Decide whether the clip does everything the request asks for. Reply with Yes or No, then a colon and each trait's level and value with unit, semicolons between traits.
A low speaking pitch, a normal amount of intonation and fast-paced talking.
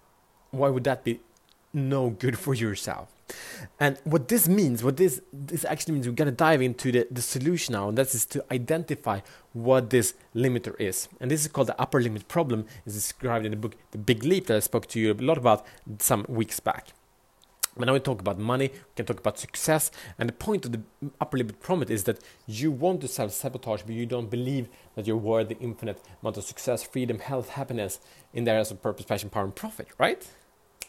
Yes: low, 125 Hz; average, 3.9 semitones; fast, 220 wpm